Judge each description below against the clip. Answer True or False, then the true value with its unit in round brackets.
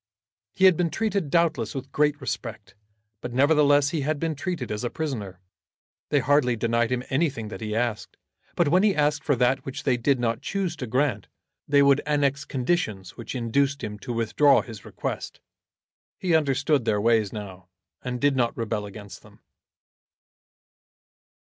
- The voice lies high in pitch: False (135 Hz)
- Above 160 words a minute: True (170 wpm)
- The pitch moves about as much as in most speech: True (4.4 semitones)